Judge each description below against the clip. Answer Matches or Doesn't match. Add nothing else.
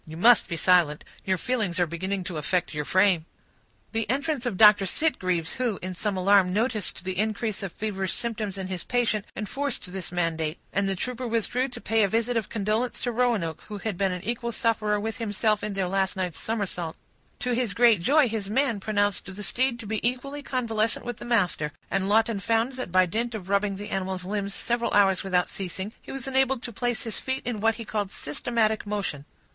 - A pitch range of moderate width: Matches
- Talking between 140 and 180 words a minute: Doesn't match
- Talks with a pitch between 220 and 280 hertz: Doesn't match